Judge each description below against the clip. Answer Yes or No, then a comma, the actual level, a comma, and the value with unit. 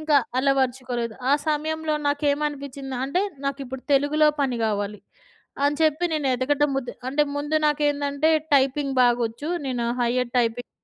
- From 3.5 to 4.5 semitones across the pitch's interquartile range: No, average, 2.7 semitones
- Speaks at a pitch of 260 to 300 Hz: Yes, very high, 275 Hz